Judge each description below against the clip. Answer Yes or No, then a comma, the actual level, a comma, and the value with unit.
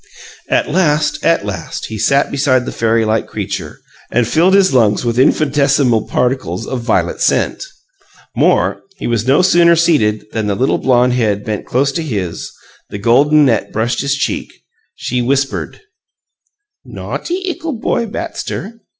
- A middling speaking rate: Yes, average, 150 wpm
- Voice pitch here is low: Yes, low, 130 Hz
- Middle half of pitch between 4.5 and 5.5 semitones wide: Yes, average, 5.1 semitones